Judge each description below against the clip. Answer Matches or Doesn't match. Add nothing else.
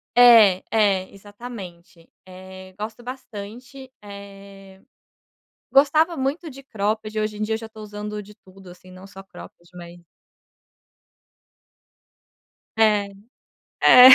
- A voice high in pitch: Matches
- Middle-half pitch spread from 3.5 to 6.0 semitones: Doesn't match